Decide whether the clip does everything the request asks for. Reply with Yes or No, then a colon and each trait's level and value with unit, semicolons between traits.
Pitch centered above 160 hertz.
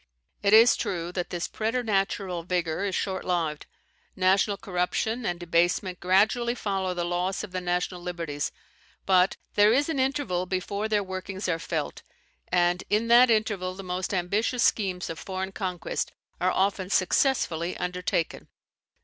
Yes: medium, 185 Hz